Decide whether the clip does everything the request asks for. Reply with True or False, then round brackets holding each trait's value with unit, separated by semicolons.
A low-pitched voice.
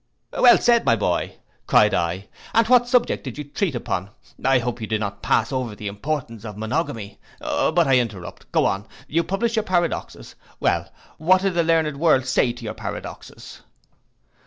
True (130 Hz)